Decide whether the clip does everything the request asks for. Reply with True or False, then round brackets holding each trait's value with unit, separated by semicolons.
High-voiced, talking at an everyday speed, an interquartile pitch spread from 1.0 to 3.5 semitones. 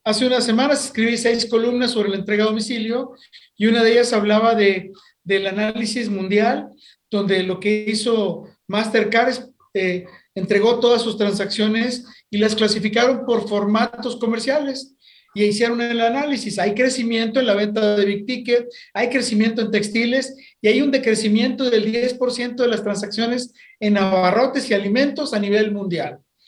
True (225 Hz; 155 wpm; 2.7 semitones)